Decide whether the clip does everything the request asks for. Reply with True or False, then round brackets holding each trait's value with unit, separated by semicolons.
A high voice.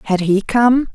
True (220 Hz)